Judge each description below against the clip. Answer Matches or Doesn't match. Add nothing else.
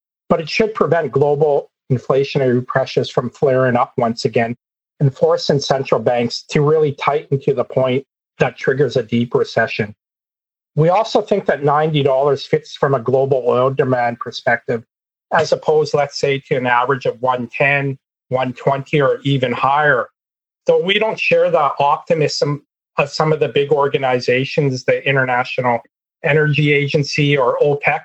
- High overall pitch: Doesn't match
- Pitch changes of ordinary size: Matches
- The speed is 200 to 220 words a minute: Doesn't match